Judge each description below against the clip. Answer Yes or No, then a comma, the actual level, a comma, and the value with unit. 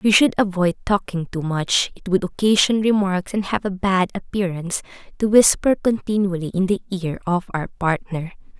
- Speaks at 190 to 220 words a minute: No, average, 170 wpm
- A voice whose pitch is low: No, high, 190 Hz